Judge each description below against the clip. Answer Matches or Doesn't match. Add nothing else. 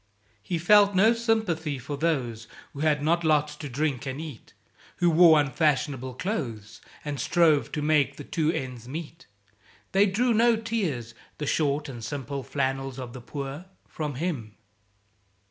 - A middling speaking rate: Matches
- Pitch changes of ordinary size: Matches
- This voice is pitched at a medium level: Matches